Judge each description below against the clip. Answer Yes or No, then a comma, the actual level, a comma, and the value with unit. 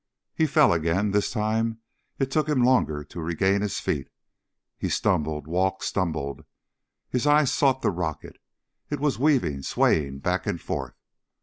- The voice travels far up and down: Yes, wide, 8.6 semitones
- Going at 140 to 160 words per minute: Yes, average, 150 wpm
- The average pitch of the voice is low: Yes, very low, 95 Hz